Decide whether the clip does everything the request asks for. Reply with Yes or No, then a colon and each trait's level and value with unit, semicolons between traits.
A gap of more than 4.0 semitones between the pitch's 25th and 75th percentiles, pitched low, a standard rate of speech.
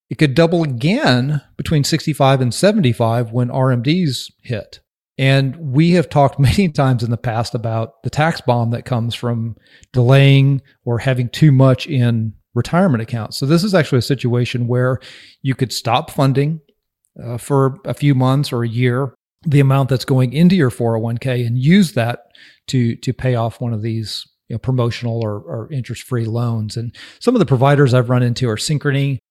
No: average, 3.1 semitones; low, 130 Hz; average, 180 wpm